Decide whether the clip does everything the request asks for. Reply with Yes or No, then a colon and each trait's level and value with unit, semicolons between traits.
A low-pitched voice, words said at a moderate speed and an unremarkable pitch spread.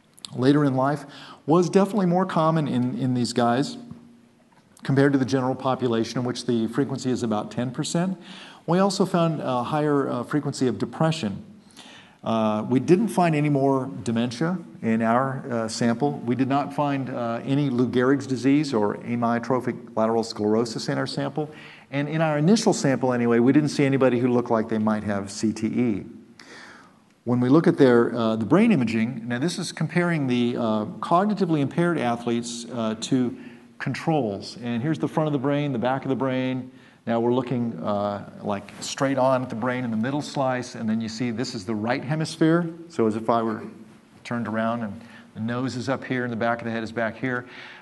Yes: low, 130 Hz; average, 195 wpm; average, 3.9 semitones